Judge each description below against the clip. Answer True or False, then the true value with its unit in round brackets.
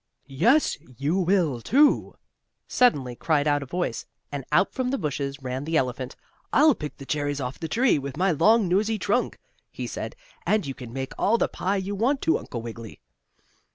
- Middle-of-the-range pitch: True (155 Hz)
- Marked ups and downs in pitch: True (7.4 semitones)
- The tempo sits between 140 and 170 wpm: False (190 wpm)